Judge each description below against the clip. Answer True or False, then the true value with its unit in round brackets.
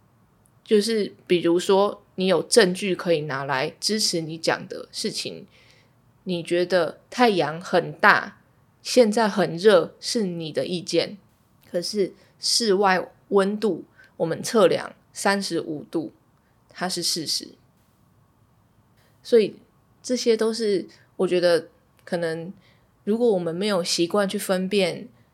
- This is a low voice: False (180 Hz)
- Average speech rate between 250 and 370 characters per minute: False (180 characters per minute)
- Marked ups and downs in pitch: False (3.6 semitones)